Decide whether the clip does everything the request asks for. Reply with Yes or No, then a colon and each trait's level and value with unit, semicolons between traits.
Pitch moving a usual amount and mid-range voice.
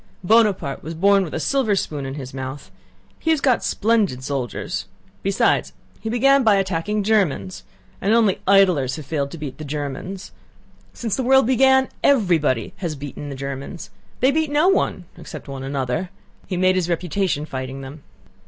No: wide, 7.8 semitones; medium, 175 Hz